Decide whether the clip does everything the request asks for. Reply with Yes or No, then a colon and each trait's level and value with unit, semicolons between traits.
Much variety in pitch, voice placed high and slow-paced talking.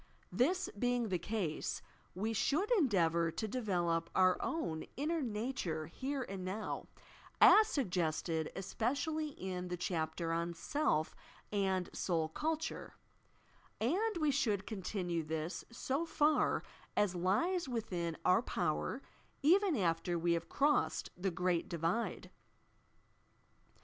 Yes: wide, 8.1 semitones; high, 195 Hz; slow, 120 wpm